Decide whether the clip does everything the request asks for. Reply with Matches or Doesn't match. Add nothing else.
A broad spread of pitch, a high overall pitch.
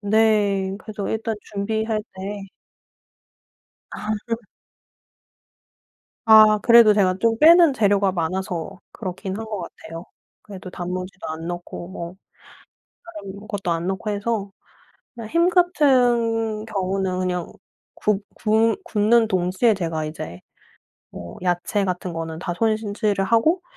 Doesn't match